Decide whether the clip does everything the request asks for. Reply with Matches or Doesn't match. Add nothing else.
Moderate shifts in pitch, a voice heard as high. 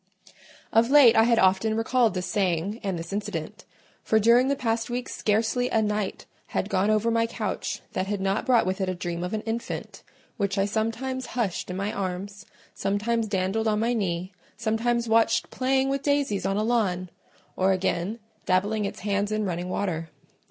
Matches